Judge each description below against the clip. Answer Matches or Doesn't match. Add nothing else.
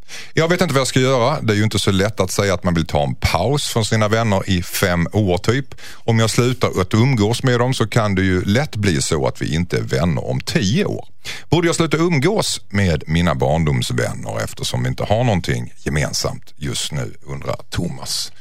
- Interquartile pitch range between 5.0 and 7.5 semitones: Matches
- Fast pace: Matches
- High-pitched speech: Doesn't match